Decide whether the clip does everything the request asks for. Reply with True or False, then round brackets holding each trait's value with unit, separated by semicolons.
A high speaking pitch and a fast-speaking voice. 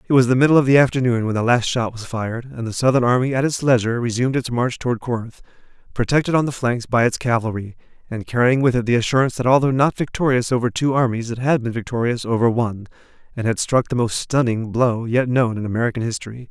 False (120 Hz; 230 wpm)